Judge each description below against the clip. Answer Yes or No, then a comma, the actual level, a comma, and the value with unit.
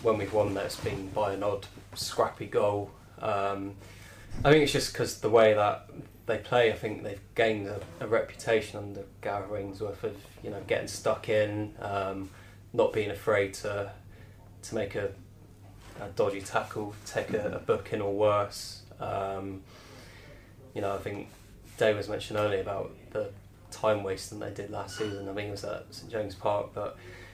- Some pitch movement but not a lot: No, narrow, 1.2 semitones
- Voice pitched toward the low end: Yes, low, 100 Hz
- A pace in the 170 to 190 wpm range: Yes, average, 180 wpm